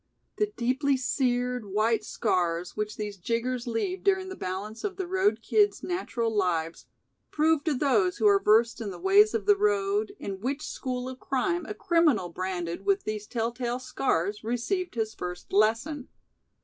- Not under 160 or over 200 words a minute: Yes, average, 170 wpm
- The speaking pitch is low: No, very high, 250 Hz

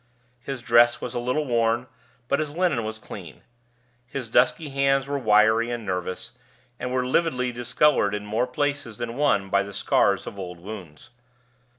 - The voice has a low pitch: Yes, low, 120 Hz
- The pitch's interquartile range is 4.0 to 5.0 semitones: Yes, average, 4.3 semitones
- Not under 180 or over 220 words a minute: No, average, 170 wpm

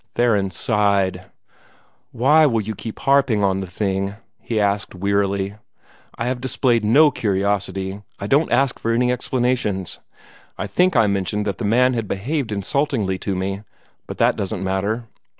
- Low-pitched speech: Yes, low, 105 Hz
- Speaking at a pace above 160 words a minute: No, average, 155 wpm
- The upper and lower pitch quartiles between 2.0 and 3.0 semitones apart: No, average, 4.0 semitones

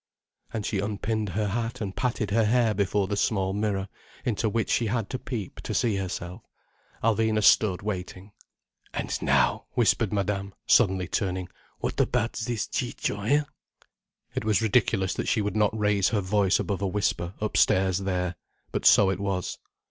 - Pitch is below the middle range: Yes, low, 105 Hz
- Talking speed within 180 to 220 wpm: No, average, 165 wpm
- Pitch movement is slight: Yes, narrow, 2.3 semitones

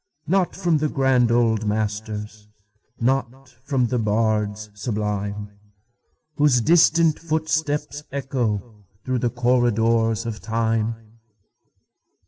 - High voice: No, low, 115 Hz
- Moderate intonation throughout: Yes, average, 4.1 semitones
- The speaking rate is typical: No, slow, 85 wpm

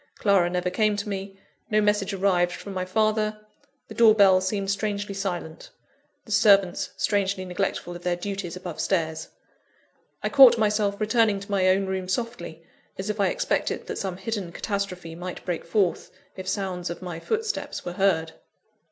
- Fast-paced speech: No, average, 170 wpm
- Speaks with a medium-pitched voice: No, high, 195 Hz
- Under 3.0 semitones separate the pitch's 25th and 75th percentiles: Yes, narrow, 2.5 semitones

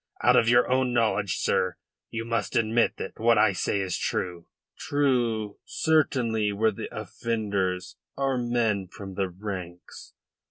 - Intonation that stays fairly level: No, average, 3.5 semitones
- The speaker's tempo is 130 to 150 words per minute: Yes, average, 145 wpm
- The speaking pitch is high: No, low, 110 Hz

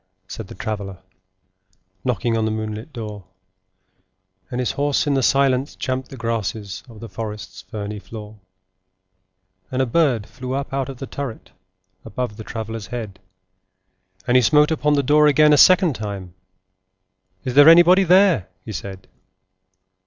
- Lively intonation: No, average, 4.8 semitones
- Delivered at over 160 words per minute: No, average, 155 wpm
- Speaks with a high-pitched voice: No, low, 120 Hz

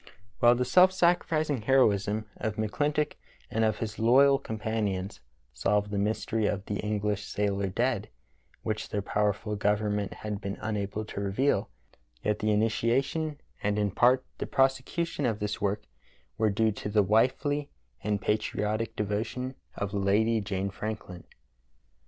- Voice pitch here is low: Yes, low, 105 Hz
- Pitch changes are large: No, average, 3.1 semitones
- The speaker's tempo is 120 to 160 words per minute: Yes, average, 145 wpm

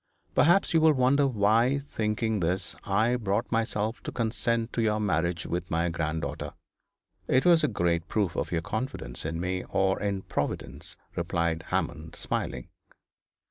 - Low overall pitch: Yes, low, 105 Hz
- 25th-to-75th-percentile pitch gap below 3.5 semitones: No, wide, 5.6 semitones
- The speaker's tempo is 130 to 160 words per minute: Yes, average, 150 wpm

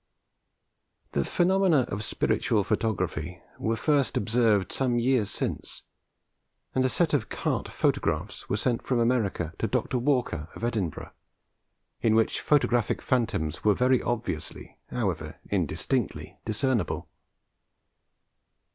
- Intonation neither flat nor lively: Yes, average, 3.9 semitones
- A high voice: No, low, 115 Hz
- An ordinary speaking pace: No, slow, 115 wpm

